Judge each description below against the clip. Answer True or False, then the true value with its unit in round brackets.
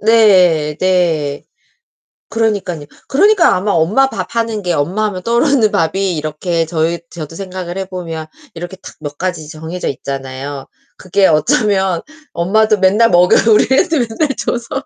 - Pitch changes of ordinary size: True (5.0 semitones)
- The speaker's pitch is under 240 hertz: True (185 Hz)